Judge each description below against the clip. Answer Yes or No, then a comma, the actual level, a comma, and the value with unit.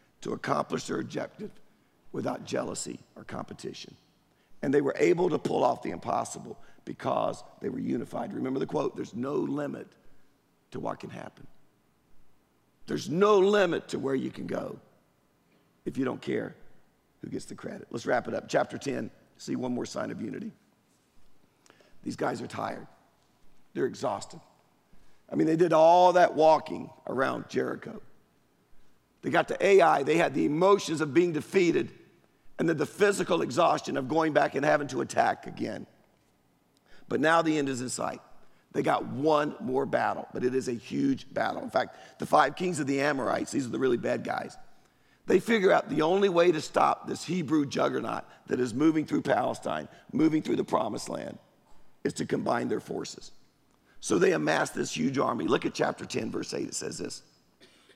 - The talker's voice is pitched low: No, medium, 165 Hz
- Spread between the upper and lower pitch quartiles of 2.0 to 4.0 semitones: No, average, 5.1 semitones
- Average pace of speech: Yes, average, 175 wpm